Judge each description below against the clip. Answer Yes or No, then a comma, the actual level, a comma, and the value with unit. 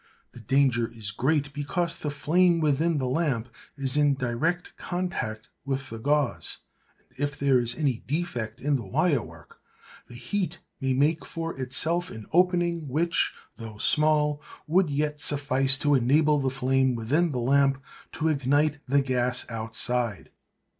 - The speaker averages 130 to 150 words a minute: Yes, average, 145 wpm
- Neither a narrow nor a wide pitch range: Yes, average, 3.8 semitones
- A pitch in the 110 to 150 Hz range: Yes, medium, 140 Hz